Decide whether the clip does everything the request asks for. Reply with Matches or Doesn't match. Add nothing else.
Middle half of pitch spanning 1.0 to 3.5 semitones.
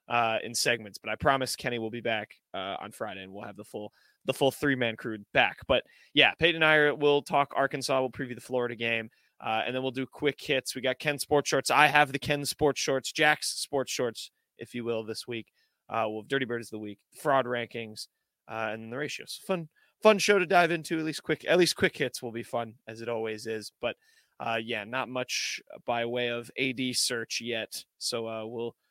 Doesn't match